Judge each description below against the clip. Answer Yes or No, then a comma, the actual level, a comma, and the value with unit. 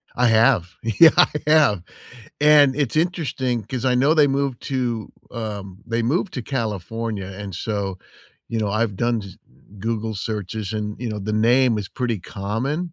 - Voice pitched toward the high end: No, low, 115 Hz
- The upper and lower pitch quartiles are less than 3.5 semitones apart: No, average, 4.0 semitones